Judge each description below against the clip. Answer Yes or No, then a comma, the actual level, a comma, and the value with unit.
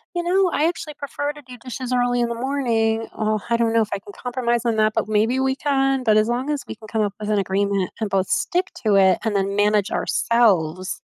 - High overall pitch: Yes, high, 230 Hz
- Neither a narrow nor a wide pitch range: Yes, average, 4.1 semitones